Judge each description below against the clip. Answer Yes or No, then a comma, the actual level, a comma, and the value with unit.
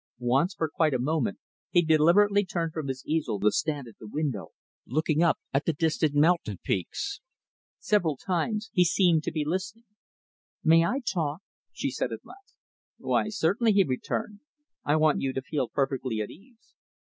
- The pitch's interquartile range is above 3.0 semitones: Yes, average, 5.1 semitones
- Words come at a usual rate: Yes, average, 175 wpm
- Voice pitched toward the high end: No, medium, 160 Hz